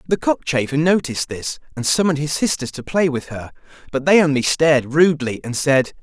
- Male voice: Yes, male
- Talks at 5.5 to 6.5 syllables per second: Yes, 5.8 syllables/s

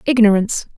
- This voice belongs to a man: No, female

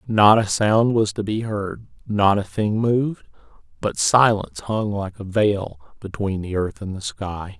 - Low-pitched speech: Yes, low, 105 Hz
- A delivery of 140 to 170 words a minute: No, average, 180 wpm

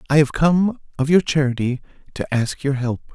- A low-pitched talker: No, medium, 145 Hz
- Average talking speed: Yes, average, 190 wpm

